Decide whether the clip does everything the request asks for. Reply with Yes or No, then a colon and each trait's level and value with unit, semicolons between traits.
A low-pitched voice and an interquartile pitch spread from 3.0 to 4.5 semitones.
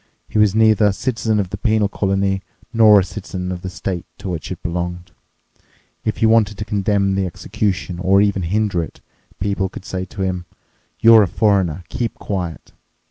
No: low, 100 Hz; narrow, 2.5 semitones